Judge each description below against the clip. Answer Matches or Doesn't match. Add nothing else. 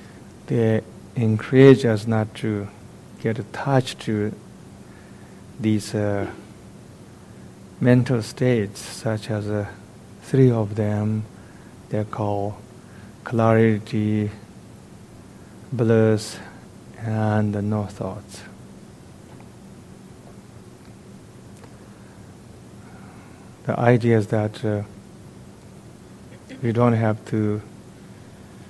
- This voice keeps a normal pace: Doesn't match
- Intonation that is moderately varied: Doesn't match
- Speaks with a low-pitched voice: Matches